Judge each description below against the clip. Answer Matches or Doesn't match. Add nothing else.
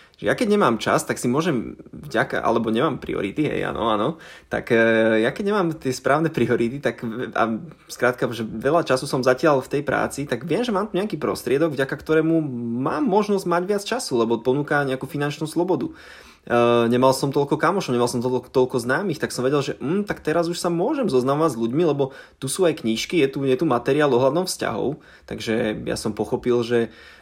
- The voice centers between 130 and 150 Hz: Matches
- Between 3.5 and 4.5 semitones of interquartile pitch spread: Doesn't match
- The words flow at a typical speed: Doesn't match